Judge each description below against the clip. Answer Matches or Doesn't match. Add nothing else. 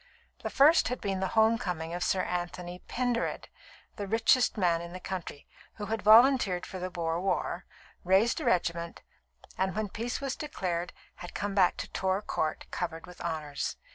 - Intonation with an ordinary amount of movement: Matches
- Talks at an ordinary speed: Matches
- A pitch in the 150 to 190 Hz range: Matches